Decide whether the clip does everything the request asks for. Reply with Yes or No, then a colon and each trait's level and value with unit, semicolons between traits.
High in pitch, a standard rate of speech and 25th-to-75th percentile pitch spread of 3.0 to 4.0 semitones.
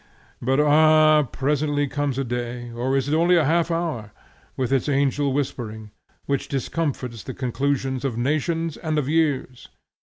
No: medium, 140 Hz; average, 155 wpm; average, 3.3 semitones